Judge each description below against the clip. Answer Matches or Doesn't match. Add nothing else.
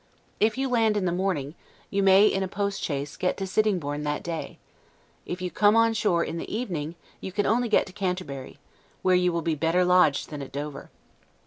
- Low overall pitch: Doesn't match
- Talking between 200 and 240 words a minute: Matches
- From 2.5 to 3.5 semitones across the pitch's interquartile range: Doesn't match